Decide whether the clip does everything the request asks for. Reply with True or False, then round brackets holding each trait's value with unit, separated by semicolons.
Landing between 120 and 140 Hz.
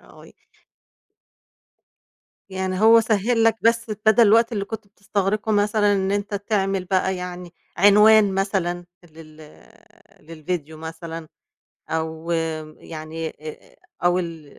False (190 Hz)